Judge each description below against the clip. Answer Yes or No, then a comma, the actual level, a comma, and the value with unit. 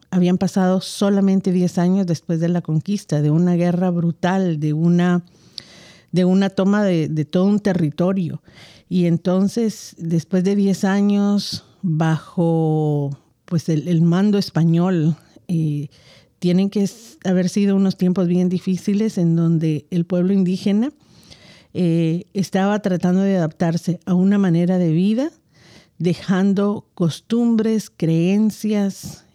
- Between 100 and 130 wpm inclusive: Yes, slow, 125 wpm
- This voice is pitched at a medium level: Yes, medium, 180 Hz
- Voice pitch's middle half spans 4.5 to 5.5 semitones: No, narrow, 2.6 semitones